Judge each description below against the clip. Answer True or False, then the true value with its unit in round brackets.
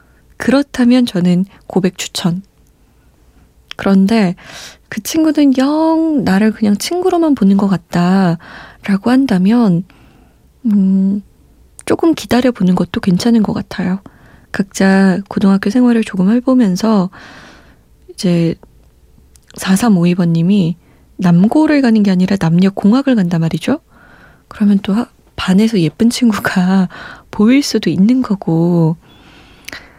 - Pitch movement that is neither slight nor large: True (4.6 semitones)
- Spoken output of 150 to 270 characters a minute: True (225 characters per minute)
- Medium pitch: False (200 Hz)